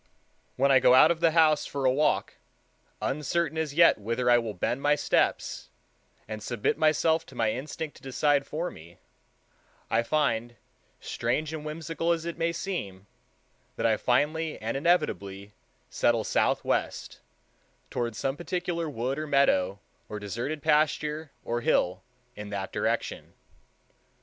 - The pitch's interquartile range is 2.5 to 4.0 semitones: No, wide, 5.5 semitones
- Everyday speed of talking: Yes, average, 145 wpm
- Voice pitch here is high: No, medium, 140 Hz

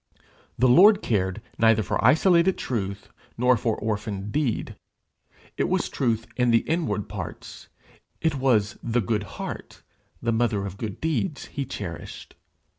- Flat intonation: No, average, 4.6 semitones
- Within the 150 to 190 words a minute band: No, average, 140 wpm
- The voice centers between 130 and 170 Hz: No, low, 115 Hz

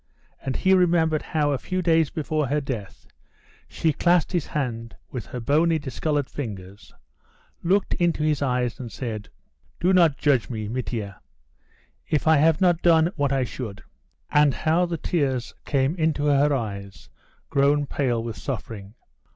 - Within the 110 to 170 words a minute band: Yes, average, 155 wpm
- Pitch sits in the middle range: Yes, medium, 145 Hz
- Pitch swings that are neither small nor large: Yes, average, 4.9 semitones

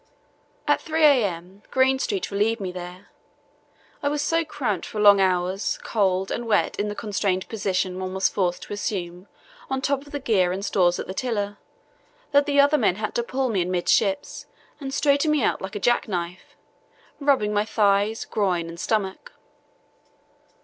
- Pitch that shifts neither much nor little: No, wide, 5.9 semitones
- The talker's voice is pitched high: Yes, high, 205 Hz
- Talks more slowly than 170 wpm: No, average, 175 wpm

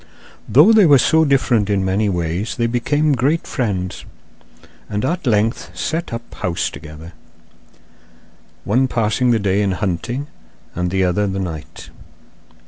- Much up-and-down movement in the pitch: Yes, wide, 5.9 semitones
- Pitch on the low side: Yes, low, 105 Hz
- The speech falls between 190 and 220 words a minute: No, average, 140 wpm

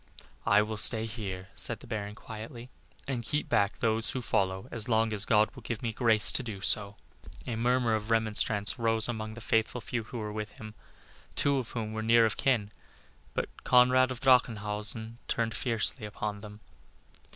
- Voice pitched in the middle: No, low, 110 Hz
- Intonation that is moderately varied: No, narrow, 1.9 semitones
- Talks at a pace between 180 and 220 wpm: Yes, average, 185 wpm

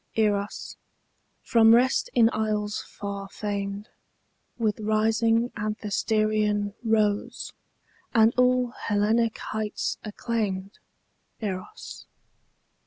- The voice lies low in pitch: No, high, 215 Hz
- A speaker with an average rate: No, slow, 80 wpm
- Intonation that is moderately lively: No, narrow, 1.6 semitones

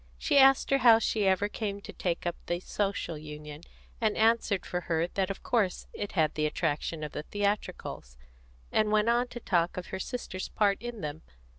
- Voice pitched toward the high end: Yes, high, 195 Hz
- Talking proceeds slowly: No, average, 195 wpm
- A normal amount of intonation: Yes, average, 4.7 semitones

